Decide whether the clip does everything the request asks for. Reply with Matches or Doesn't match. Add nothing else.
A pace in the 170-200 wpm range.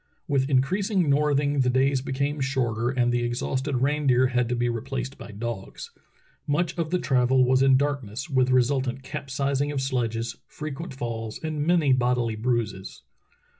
Doesn't match